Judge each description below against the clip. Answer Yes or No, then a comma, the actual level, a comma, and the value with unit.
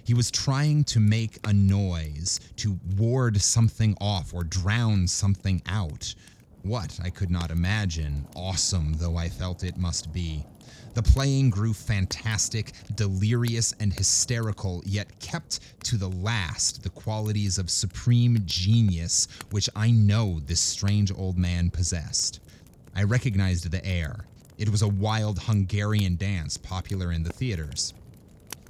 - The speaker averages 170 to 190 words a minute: No, average, 140 wpm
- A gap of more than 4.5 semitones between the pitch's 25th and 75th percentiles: No, average, 3.7 semitones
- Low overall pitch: Yes, low, 100 Hz